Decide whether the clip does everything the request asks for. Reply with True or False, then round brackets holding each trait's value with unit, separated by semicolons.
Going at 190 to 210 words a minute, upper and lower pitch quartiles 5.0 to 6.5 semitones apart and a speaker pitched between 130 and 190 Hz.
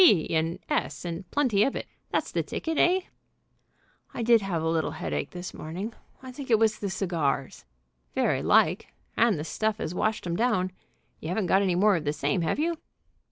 True (200 wpm; 5.4 semitones; 185 Hz)